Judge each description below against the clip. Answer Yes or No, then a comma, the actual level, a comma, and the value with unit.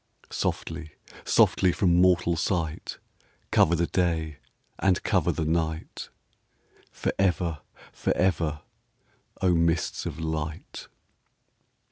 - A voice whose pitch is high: No, very low, 85 Hz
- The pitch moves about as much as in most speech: No, narrow, 1.9 semitones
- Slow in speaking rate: Yes, slow, 90 wpm